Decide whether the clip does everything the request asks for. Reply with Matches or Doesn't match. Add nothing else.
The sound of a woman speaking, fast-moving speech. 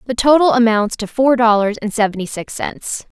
Doesn't match